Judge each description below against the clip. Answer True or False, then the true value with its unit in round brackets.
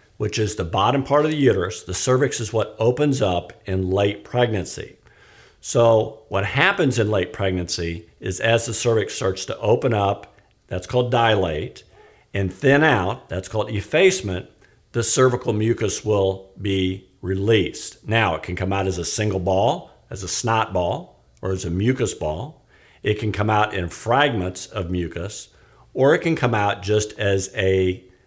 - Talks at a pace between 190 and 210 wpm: False (170 wpm)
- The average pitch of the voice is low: True (105 Hz)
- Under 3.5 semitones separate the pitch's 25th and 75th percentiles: False (3.8 semitones)